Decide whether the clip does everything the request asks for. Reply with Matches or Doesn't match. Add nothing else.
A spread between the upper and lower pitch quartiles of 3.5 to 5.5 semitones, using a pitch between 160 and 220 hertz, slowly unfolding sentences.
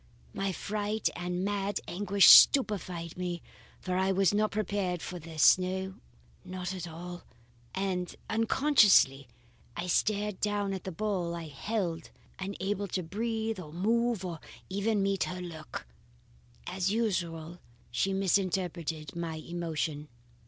Doesn't match